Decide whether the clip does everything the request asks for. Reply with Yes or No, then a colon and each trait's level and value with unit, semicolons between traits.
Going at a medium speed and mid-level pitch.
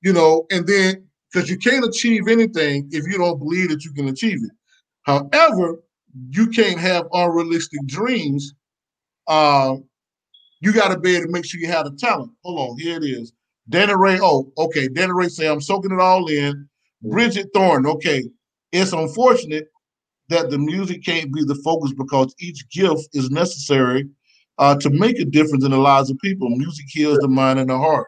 Yes: average, 190 wpm; medium, 160 Hz